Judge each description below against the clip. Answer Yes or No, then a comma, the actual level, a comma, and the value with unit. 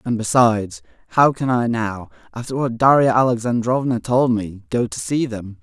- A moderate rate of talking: Yes, average, 170 wpm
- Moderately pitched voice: No, low, 115 Hz